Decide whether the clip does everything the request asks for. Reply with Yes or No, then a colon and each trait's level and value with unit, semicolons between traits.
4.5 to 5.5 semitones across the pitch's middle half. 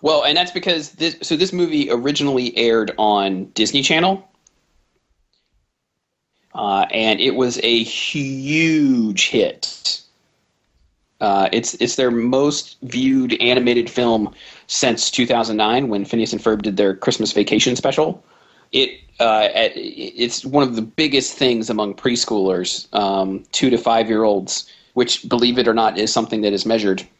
Yes: average, 5.1 semitones